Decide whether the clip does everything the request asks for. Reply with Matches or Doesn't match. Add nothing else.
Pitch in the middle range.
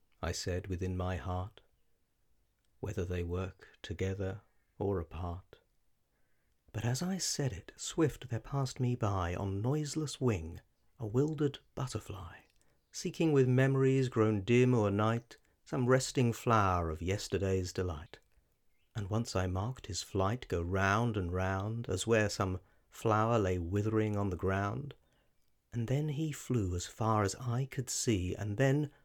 Doesn't match